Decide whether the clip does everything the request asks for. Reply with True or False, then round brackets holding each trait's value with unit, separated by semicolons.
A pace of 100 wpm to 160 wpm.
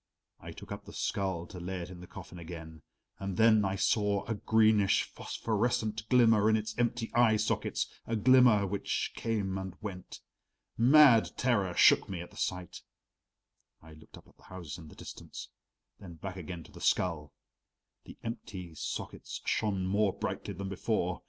False (170 wpm)